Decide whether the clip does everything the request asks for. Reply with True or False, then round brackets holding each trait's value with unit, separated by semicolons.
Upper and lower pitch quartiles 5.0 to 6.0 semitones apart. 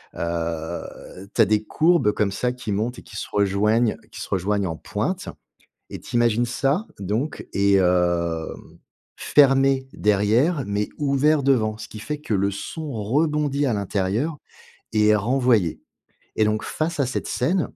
True (5.5 semitones)